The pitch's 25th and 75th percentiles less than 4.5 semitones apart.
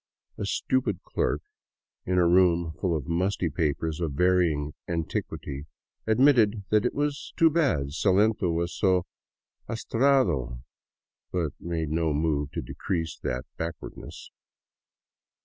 No: average, 4.8 semitones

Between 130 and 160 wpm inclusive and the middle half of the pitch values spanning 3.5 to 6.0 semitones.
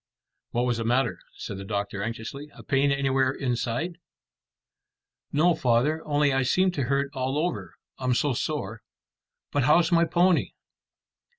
Yes: average, 150 wpm; average, 4.2 semitones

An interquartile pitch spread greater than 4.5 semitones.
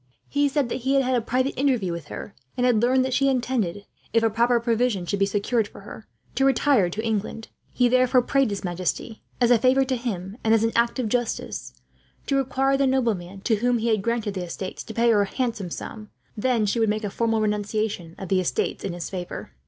No: average, 3.8 semitones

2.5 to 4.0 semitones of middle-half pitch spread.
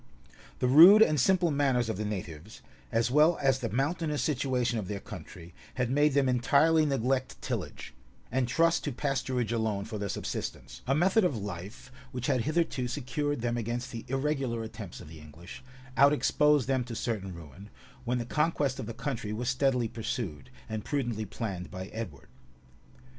No: average, 4.4 semitones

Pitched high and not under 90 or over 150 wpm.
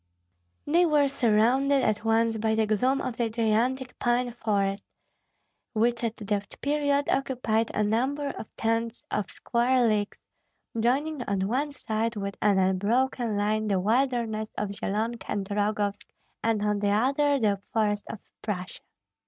Yes: high, 225 Hz; average, 145 wpm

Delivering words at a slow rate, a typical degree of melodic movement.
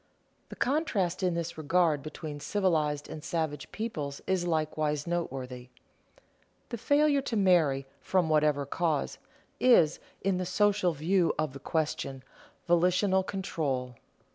Yes: slow, 125 wpm; average, 4.2 semitones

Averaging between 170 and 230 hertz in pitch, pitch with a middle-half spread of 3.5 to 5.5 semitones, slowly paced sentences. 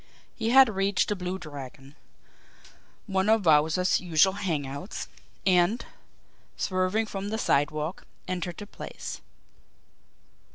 Yes: medium, 185 Hz; average, 4.4 semitones; slow, 115 wpm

